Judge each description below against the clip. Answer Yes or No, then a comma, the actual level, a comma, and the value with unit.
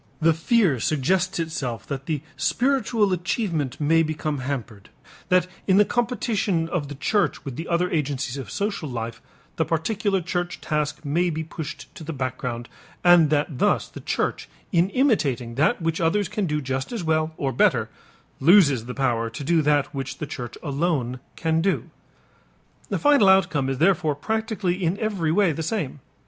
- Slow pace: No, average, 170 wpm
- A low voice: No, medium, 160 Hz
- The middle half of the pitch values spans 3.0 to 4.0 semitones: No, average, 5.1 semitones